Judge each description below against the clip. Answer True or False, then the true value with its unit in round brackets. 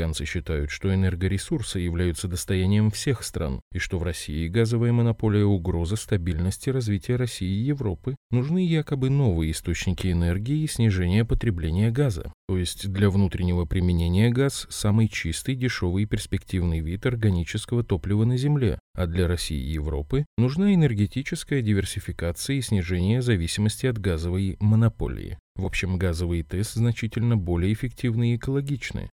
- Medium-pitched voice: False (100 Hz)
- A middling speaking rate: True (140 wpm)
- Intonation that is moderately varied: True (4.9 semitones)